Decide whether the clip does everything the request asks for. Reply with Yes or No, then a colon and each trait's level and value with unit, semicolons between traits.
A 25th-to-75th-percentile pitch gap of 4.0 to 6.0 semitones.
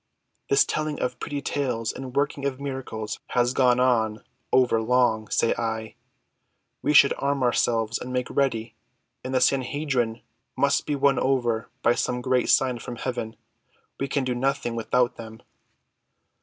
No: average, 2.9 semitones